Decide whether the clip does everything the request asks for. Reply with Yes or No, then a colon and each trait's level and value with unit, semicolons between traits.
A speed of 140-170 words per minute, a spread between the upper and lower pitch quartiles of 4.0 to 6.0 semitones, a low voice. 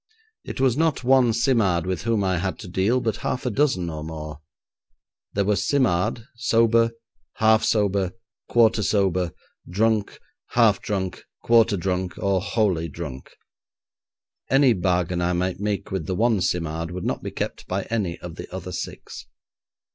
Yes: average, 155 wpm; average, 4.4 semitones; low, 100 Hz